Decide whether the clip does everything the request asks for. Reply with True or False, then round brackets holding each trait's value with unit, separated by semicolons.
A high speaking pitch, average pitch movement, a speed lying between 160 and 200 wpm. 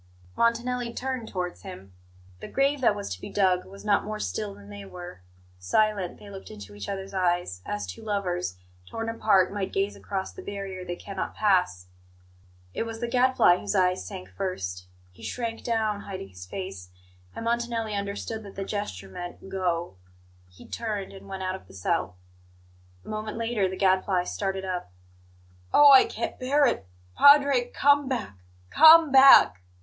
True (195 Hz; 4.3 semitones; 170 wpm)